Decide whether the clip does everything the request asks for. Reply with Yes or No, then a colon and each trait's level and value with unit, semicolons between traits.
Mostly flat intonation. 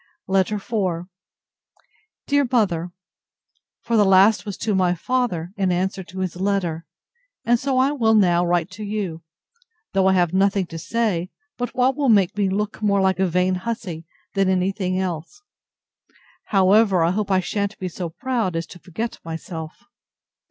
No: average, 3.2 semitones